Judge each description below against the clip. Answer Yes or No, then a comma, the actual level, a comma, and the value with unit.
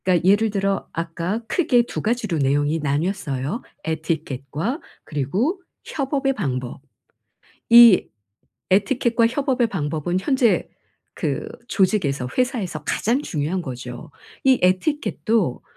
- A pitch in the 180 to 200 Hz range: Yes, high, 190 Hz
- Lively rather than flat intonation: Yes, wide, 7.9 semitones